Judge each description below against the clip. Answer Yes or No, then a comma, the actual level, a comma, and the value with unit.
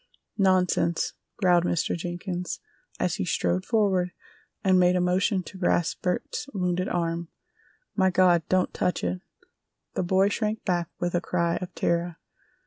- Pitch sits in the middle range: Yes, medium, 180 Hz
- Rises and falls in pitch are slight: Yes, narrow, 1.4 semitones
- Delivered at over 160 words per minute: No, average, 145 wpm